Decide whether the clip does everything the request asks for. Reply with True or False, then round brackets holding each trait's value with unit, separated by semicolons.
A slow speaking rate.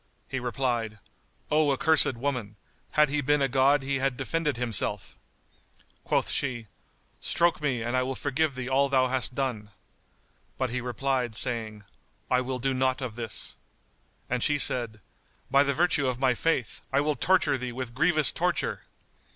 False (165 wpm)